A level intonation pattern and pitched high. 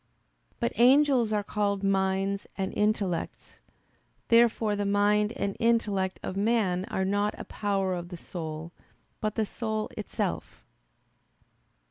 Yes: narrow, 2.2 semitones; high, 205 Hz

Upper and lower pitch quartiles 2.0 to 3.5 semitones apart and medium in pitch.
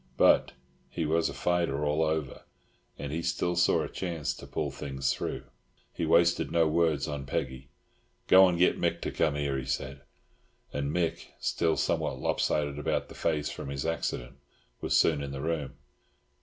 No: average, 3.2 semitones; very low, 75 Hz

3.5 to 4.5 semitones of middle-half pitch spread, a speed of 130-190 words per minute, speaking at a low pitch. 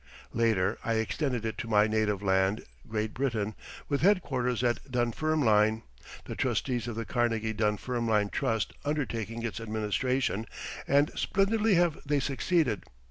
Yes: average, 4.0 semitones; slow, 135 wpm; low, 115 Hz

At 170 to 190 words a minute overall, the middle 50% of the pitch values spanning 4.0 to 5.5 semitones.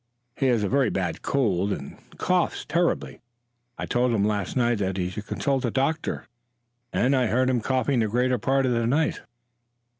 Yes: average, 185 wpm; average, 4.4 semitones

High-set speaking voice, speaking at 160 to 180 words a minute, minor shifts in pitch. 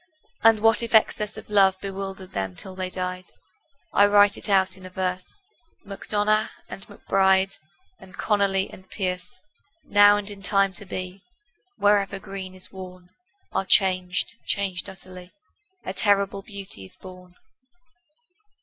No: high, 195 Hz; average, 140 wpm; narrow, 1.6 semitones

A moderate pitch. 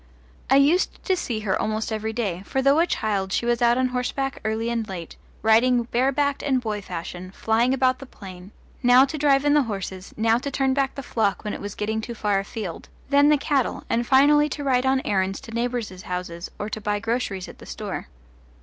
No: high, 235 Hz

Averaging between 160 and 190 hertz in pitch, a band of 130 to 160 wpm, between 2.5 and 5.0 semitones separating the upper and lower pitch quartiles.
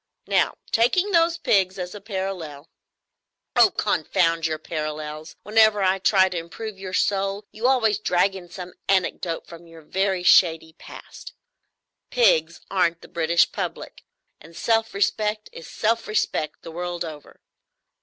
Yes: medium, 185 Hz; average, 145 wpm; average, 4.1 semitones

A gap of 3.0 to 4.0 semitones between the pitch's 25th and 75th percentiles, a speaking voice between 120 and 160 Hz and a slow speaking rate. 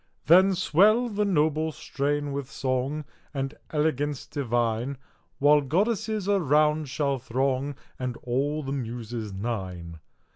Yes: average, 3.7 semitones; medium, 140 Hz; slow, 115 wpm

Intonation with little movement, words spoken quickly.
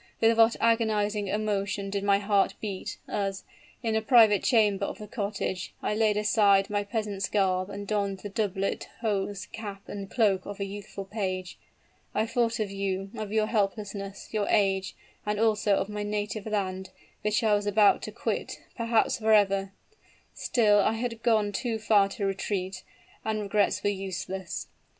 No: narrow, 1.7 semitones; average, 165 wpm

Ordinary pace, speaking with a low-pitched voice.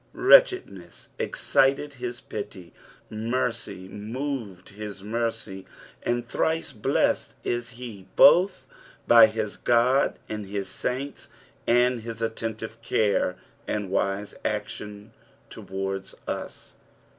No: slow, 100 wpm; low, 110 Hz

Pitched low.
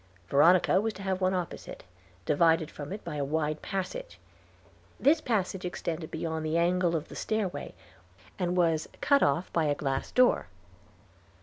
No: medium, 175 Hz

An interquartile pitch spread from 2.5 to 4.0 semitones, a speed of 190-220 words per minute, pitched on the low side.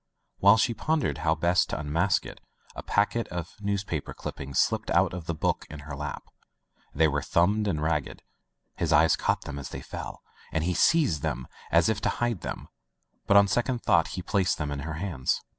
No: average, 5.1 semitones; average, 200 wpm; very low, 85 Hz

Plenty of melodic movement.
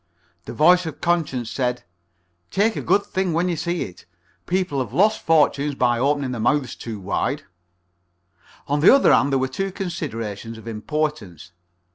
Yes: wide, 6.5 semitones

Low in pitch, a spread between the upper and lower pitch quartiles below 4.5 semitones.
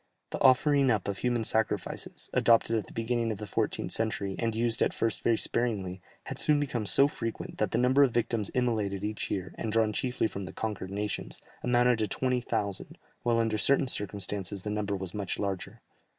Yes: low, 110 Hz; average, 3.1 semitones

